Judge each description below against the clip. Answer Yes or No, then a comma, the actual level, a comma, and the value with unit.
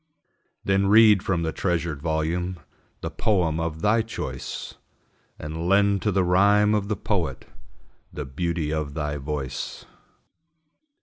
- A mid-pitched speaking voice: No, very low, 85 Hz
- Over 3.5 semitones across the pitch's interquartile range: Yes, average, 4.3 semitones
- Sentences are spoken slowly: Yes, slow, 130 wpm